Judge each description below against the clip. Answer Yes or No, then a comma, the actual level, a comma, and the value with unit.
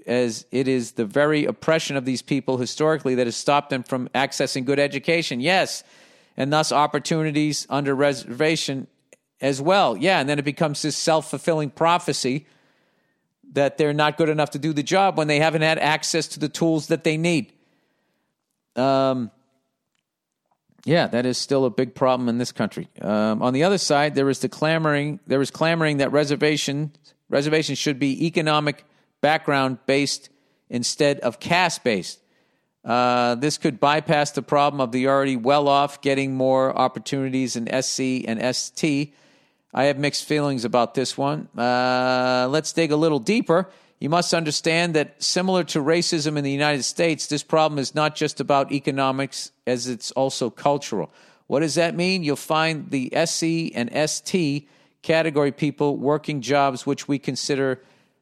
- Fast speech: No, average, 160 wpm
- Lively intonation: No, average, 2.8 semitones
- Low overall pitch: No, medium, 145 Hz